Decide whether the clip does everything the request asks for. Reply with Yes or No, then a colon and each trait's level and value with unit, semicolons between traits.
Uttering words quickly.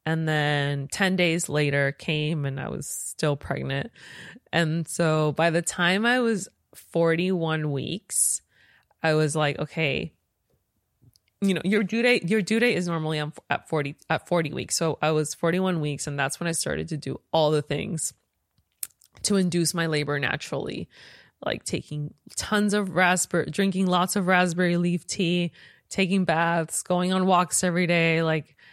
No: average, 165 wpm